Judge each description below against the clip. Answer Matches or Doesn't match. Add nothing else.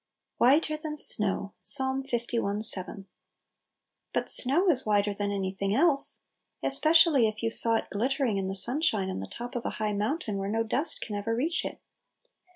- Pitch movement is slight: Doesn't match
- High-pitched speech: Matches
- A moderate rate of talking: Matches